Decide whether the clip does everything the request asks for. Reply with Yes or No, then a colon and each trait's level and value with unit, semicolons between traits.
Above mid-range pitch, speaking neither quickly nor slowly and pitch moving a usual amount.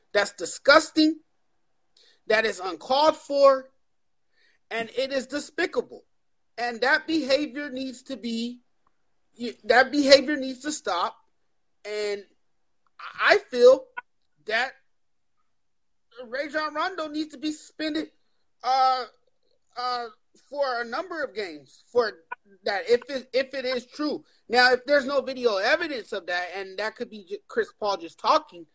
No: very high, 270 Hz; slow, 130 wpm; average, 4.6 semitones